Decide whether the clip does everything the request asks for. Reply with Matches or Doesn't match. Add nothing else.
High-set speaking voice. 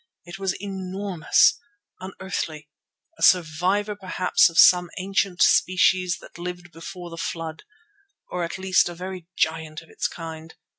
Doesn't match